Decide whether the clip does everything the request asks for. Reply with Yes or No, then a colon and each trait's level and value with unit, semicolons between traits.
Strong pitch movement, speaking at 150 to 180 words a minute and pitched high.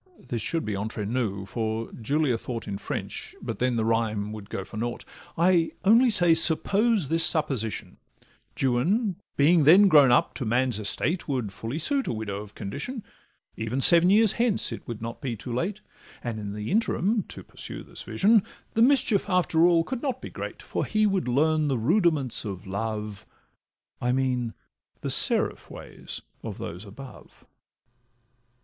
No: wide, 8.2 semitones; average, 170 wpm; low, 130 Hz